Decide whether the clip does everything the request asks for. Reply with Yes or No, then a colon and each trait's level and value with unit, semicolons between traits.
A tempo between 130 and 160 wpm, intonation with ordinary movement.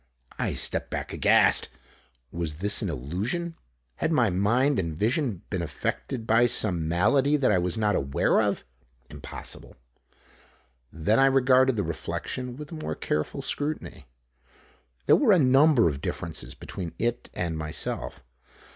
No: average, 145 wpm; wide, 7.8 semitones